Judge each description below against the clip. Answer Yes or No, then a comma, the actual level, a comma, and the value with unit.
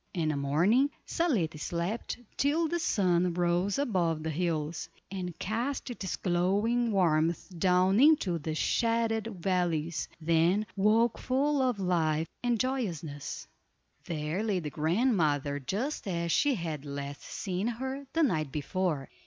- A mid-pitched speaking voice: Yes, medium, 180 Hz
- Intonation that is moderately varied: No, wide, 6.3 semitones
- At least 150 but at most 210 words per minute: No, slow, 135 wpm